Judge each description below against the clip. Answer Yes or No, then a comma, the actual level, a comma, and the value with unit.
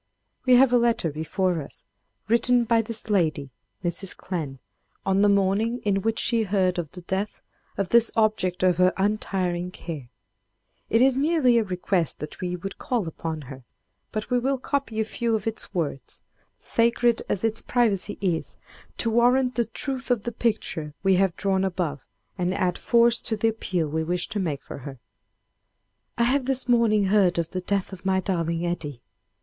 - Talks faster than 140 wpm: Yes, average, 175 wpm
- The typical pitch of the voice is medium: No, high, 195 Hz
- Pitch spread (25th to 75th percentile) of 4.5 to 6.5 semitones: Yes, average, 4.8 semitones